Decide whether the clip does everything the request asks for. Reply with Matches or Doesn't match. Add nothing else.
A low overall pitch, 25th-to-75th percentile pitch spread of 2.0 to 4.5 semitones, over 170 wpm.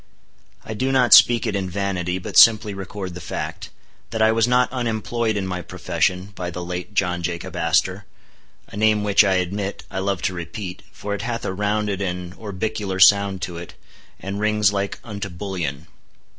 Matches